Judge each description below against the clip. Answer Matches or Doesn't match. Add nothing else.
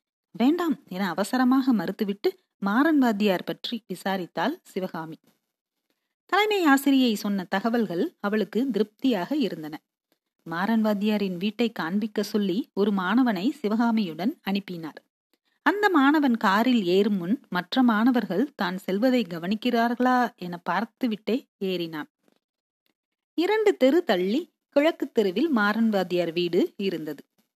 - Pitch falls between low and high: Doesn't match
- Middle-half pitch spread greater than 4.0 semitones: Matches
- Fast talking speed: Doesn't match